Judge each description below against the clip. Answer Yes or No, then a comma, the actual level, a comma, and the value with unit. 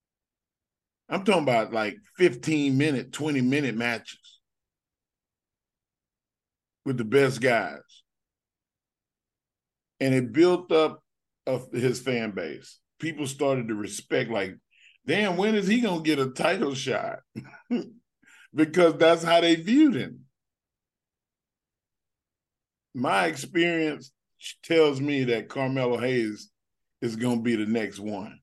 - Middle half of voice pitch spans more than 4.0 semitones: Yes, average, 5.3 semitones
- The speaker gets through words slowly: Yes, slow, 120 wpm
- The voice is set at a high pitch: No, low, 135 Hz